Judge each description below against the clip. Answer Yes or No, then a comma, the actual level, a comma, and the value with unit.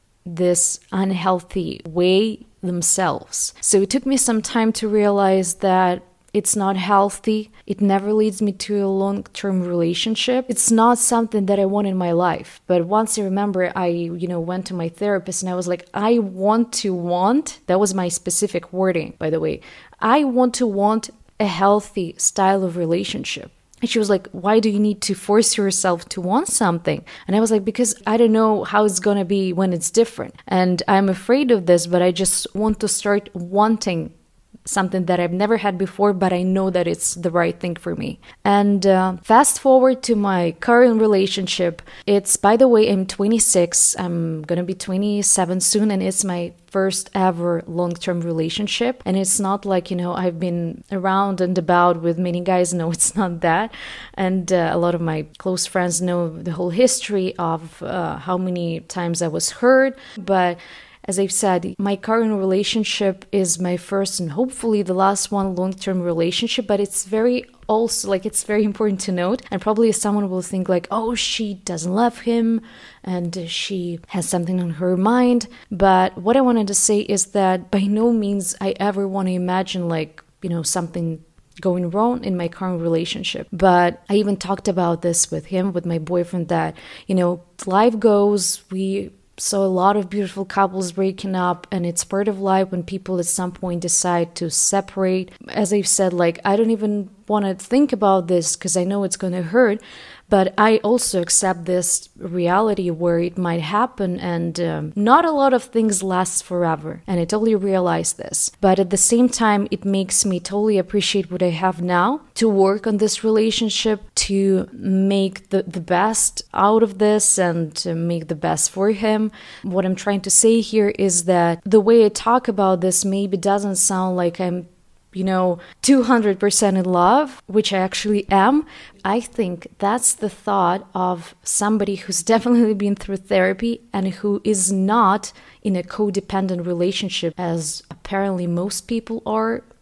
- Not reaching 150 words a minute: No, average, 185 wpm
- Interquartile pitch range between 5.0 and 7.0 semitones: No, average, 2.8 semitones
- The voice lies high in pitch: Yes, high, 195 Hz